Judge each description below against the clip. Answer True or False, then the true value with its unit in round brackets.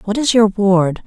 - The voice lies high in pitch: True (205 Hz)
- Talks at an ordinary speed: False (225 wpm)